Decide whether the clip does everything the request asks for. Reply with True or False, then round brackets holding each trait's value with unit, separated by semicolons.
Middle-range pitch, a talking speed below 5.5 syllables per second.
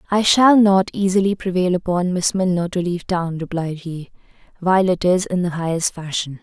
True (180 Hz; 5.3 syllables/s)